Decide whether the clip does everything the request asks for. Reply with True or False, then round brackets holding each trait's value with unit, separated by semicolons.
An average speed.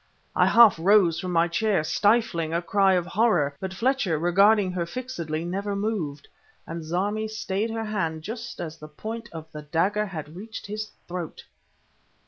True (165 wpm)